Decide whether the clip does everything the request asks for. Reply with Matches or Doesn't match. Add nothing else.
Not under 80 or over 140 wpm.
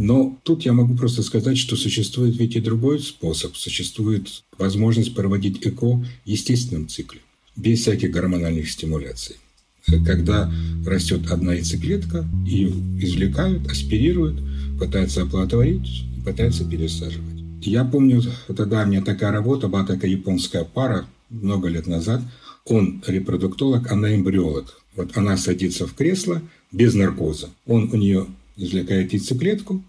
Matches